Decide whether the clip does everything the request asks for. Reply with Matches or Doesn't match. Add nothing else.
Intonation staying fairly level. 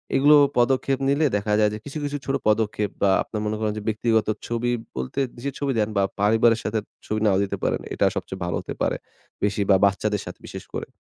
Doesn't match